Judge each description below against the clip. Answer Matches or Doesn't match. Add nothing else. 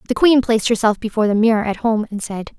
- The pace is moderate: Doesn't match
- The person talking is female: Matches